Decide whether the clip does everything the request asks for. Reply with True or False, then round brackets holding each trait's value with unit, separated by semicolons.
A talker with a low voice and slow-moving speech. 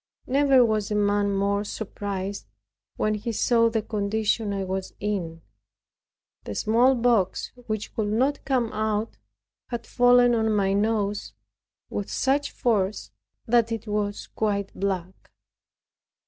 False (215 Hz; 125 wpm)